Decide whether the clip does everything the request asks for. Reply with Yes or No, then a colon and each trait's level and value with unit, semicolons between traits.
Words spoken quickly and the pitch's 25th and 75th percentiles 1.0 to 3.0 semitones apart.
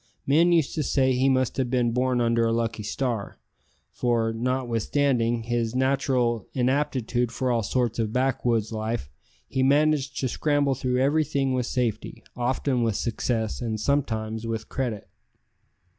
No: average, 145 wpm; narrow, 2.6 semitones